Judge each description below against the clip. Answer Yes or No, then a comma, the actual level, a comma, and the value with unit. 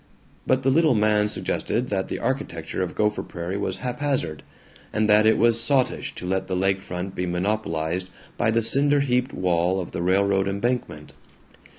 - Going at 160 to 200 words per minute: Yes, average, 175 wpm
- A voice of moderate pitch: No, low, 105 Hz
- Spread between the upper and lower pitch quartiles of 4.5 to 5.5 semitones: Yes, average, 4.8 semitones